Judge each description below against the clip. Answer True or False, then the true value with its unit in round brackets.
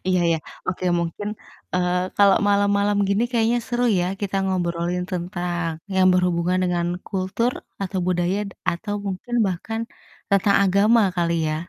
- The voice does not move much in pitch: True (2.3 semitones)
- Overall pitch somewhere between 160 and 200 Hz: True (185 Hz)